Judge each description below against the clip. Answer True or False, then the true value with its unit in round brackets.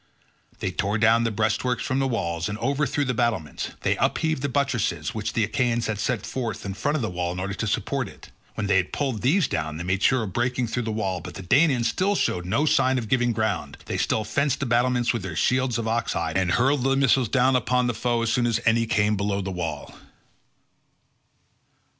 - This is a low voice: True (115 Hz)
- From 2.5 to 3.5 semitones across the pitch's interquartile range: False (4.1 semitones)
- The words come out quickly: True (225 wpm)